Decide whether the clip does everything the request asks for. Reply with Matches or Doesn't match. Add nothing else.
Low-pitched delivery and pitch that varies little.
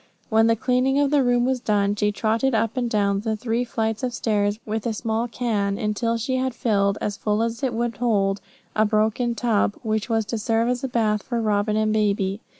Doesn't match